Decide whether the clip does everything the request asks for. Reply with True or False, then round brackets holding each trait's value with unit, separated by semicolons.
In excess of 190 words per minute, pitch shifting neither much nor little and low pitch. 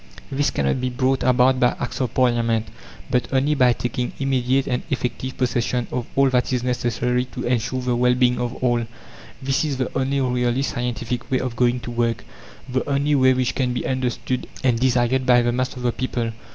False (200 wpm; 1.2 semitones; 125 Hz)